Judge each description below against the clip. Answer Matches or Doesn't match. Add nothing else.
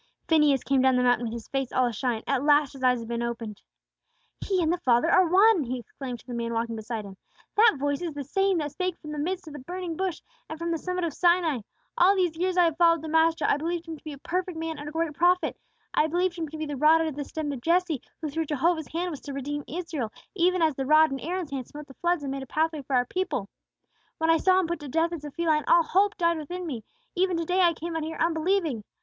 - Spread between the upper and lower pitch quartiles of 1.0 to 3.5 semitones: Doesn't match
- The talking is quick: Matches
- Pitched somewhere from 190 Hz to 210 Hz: Doesn't match